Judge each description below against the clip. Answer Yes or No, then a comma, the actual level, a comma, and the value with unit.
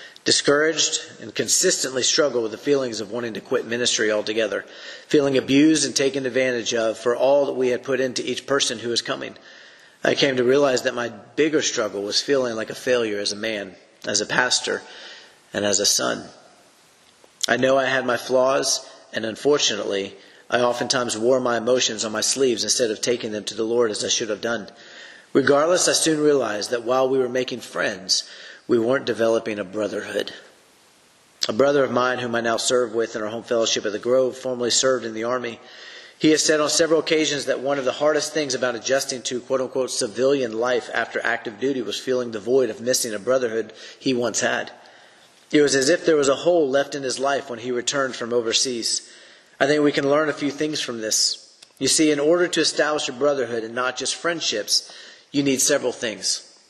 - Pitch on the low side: Yes, low, 130 Hz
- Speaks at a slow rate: No, fast, 205 wpm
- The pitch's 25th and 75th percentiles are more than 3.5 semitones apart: No, average, 3.0 semitones